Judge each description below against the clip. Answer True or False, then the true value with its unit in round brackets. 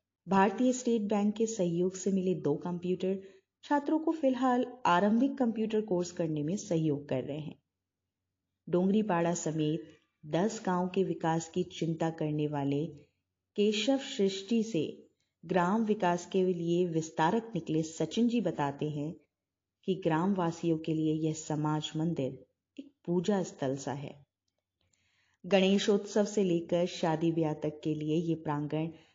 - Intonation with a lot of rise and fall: False (4.4 semitones)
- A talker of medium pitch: True (170 Hz)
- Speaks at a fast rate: False (135 wpm)